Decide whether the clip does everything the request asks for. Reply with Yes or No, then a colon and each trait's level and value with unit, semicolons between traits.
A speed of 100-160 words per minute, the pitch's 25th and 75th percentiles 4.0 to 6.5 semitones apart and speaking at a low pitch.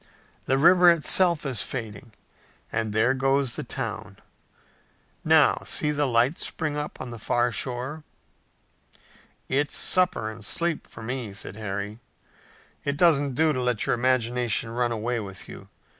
Yes: average, 145 wpm; average, 4.5 semitones; low, 125 Hz